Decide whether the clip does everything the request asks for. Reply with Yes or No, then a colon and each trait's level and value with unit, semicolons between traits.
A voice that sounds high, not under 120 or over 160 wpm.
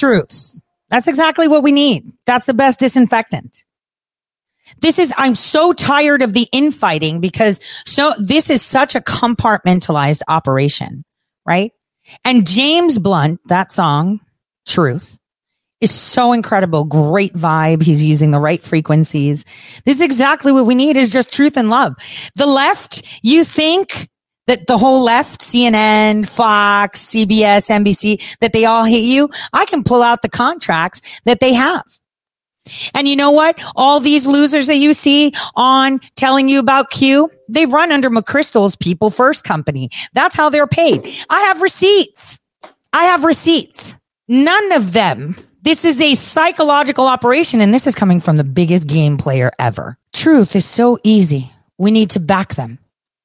Yes: high, 240 Hz; average, 155 wpm